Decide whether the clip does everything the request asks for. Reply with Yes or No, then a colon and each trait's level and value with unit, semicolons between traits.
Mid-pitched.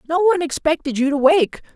No: very high, 270 Hz